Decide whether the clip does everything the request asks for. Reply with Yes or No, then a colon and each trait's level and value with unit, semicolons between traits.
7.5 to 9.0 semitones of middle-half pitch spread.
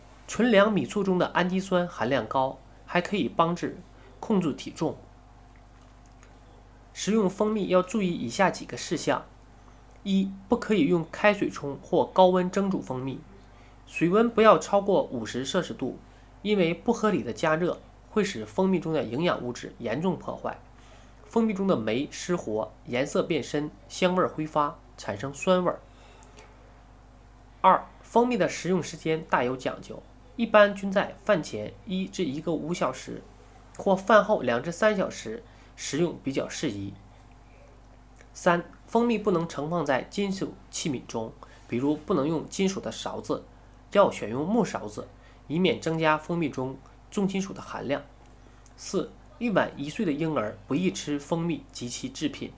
Yes: wide, 7.9 semitones